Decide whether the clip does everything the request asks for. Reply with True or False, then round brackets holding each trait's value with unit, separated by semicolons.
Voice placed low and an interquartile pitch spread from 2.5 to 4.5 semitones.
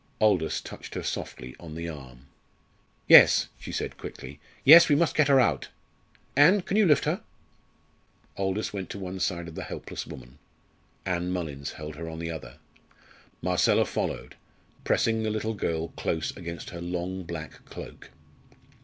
False (85 Hz; 5.3 semitones)